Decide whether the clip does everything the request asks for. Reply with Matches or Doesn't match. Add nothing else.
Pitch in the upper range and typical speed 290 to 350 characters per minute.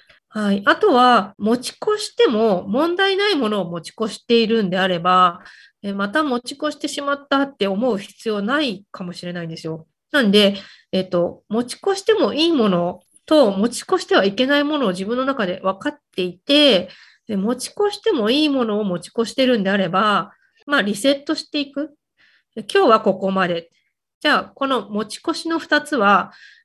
Matches